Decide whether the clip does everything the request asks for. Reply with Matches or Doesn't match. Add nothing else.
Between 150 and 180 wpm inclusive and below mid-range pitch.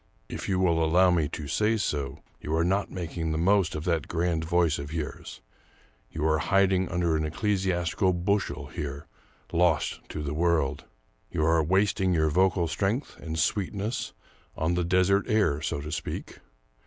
Matches